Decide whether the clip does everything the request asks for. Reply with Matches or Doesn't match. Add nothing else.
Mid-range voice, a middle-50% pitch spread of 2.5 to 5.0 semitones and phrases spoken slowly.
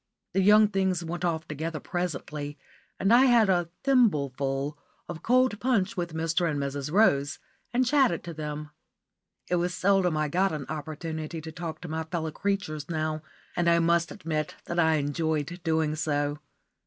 Doesn't match